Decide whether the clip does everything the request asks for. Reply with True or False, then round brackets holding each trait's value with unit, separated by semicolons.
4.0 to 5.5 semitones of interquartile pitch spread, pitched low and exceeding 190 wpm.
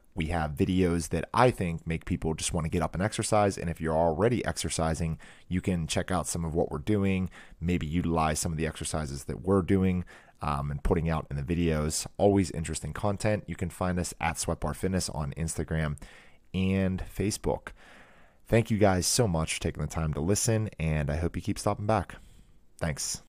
False (3.3 semitones; 85 Hz; 200 wpm)